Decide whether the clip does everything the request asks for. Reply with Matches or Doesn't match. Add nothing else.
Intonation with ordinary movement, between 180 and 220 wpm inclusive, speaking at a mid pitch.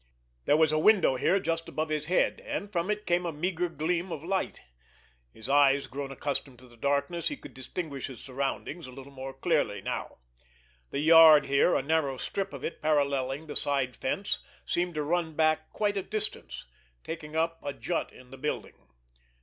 Matches